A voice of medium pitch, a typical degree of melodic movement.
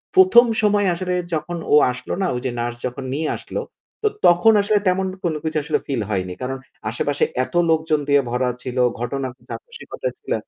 No: medium, 155 Hz; wide, 6.6 semitones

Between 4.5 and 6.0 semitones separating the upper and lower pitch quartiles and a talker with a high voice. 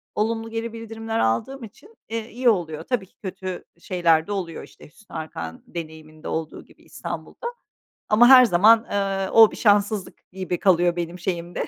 Yes: average, 4.8 semitones; high, 195 Hz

